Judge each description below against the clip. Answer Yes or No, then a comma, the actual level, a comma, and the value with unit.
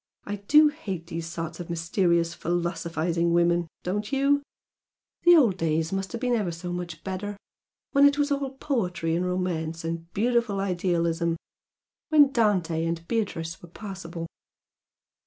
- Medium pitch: Yes, medium, 180 Hz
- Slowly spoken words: No, average, 145 wpm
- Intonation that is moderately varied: Yes, average, 4.5 semitones